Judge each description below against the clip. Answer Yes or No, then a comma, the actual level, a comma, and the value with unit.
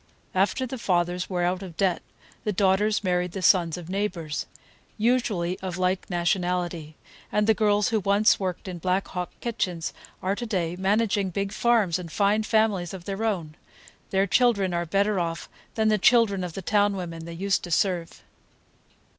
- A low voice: No, high, 190 Hz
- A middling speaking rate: Yes, average, 170 wpm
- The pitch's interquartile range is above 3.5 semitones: No, average, 2.9 semitones